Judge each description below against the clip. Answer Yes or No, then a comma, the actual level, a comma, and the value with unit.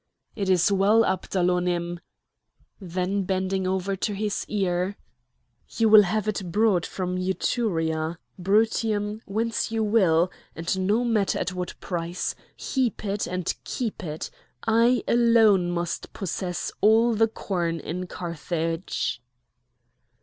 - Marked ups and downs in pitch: No, average, 3.4 semitones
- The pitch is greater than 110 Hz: Yes, high, 190 Hz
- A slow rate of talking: Yes, slow, 120 wpm